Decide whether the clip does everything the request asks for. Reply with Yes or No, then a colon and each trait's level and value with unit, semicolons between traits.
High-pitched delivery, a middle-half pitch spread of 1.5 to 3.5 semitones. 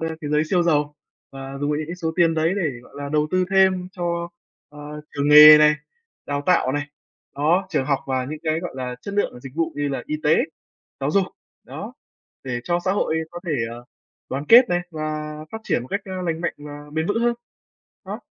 No: medium, 155 Hz; average, 3.2 semitones